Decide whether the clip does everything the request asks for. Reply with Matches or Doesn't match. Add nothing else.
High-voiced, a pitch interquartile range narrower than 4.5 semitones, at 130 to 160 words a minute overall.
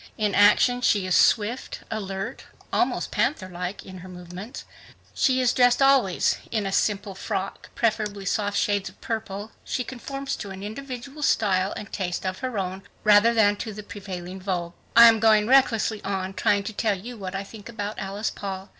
Doesn't match